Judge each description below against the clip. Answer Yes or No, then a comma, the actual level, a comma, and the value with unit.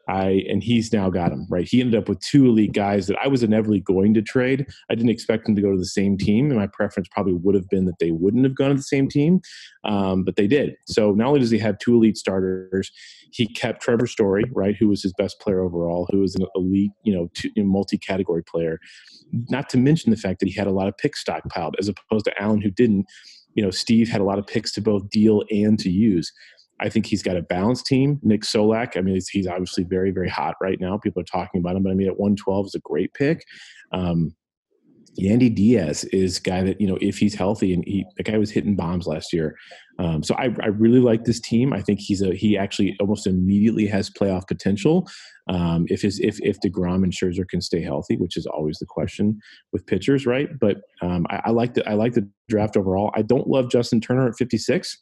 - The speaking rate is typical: No, fast, 245 wpm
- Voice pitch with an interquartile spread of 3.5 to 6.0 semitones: No, average, 3.1 semitones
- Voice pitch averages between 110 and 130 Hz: No, low, 100 Hz